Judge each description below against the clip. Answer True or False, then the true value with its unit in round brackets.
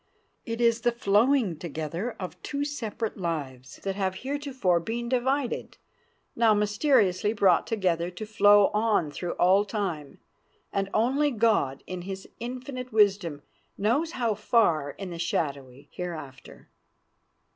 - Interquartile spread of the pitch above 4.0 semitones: True (5.4 semitones)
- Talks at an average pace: False (130 wpm)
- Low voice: False (205 Hz)